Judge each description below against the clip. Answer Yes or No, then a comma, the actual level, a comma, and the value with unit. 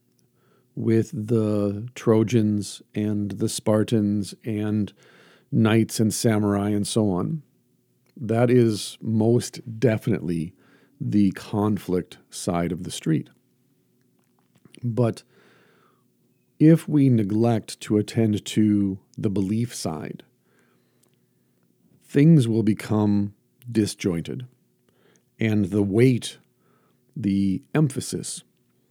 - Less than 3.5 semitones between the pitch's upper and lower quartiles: Yes, average, 2.7 semitones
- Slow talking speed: Yes, slow, 85 wpm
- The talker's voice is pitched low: Yes, low, 110 Hz